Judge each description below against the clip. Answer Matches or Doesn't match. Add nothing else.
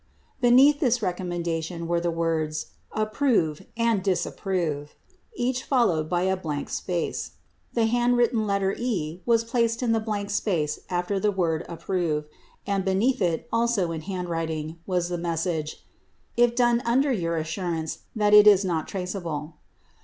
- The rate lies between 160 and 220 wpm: Doesn't match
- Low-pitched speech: Doesn't match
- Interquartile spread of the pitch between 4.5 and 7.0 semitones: Matches